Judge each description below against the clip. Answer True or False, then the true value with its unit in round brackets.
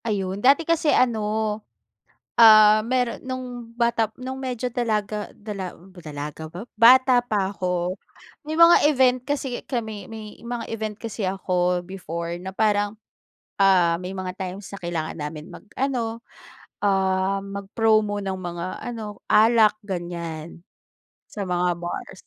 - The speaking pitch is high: True (205 Hz)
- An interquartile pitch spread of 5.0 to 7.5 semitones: False (4.2 semitones)